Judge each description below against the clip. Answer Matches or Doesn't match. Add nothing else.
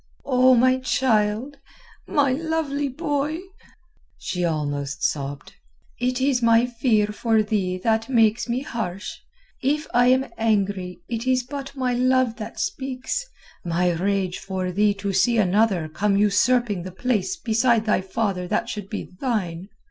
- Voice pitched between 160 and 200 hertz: Doesn't match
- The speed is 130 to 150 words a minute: Matches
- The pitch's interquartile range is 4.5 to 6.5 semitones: Matches